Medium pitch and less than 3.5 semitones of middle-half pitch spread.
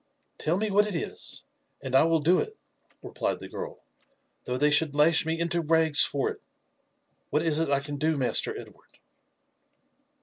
Yes: medium, 160 Hz; narrow, 2.5 semitones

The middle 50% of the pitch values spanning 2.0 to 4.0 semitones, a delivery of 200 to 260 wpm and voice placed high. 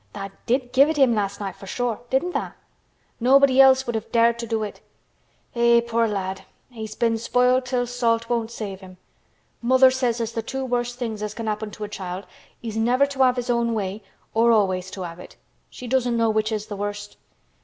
Yes: average, 2.8 semitones; fast, 205 wpm; high, 230 Hz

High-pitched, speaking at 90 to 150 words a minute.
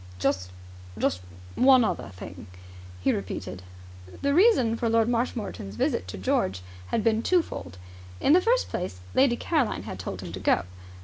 No: high, 220 Hz; average, 160 wpm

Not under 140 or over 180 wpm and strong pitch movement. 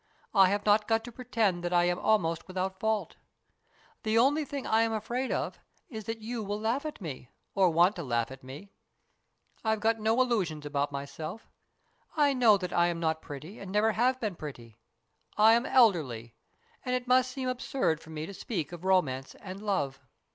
No: average, 195 wpm; wide, 5.7 semitones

